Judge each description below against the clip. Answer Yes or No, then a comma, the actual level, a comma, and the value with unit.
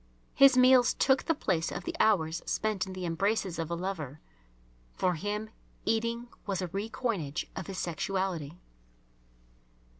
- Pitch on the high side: Yes, high, 195 Hz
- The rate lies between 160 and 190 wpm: No, average, 150 wpm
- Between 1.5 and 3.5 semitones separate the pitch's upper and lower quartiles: No, average, 4.8 semitones